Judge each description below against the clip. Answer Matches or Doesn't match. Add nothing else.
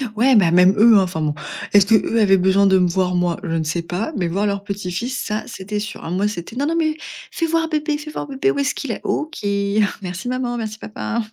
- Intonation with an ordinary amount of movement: Doesn't match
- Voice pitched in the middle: Doesn't match